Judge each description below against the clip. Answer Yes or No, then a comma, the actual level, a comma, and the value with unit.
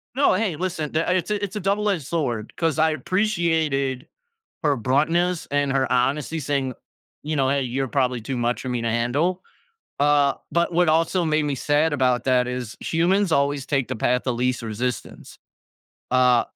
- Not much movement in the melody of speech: No, average, 4.7 semitones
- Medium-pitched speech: Yes, medium, 145 Hz